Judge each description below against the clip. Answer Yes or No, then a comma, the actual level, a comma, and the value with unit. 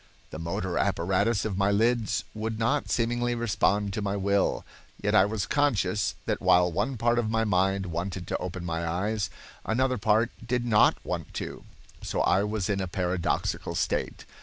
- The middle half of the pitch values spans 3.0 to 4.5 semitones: Yes, average, 3.3 semitones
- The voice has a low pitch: Yes, low, 105 Hz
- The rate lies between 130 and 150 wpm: No, average, 175 wpm